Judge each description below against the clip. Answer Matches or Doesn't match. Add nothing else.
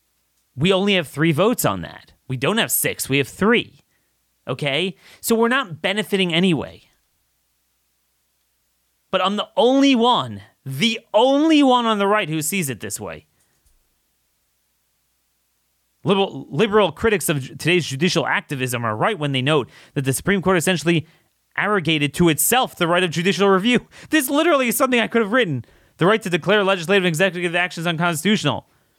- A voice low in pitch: Doesn't match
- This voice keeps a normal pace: Matches